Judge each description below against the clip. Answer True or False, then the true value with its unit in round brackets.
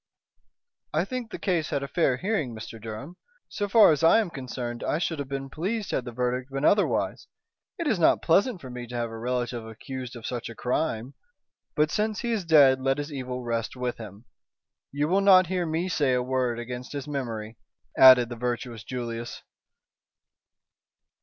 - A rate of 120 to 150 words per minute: False (190 wpm)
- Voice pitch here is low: True (130 Hz)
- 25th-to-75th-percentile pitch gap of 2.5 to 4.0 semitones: False (5.3 semitones)